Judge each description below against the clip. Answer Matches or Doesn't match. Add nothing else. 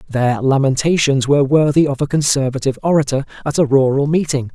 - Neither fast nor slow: Matches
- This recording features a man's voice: Matches